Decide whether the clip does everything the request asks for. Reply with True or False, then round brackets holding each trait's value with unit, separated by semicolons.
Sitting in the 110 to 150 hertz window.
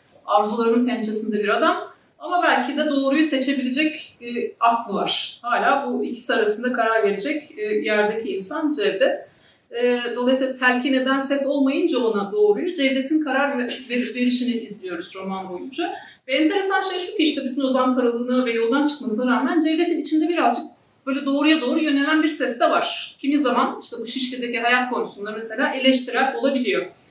False (265 Hz)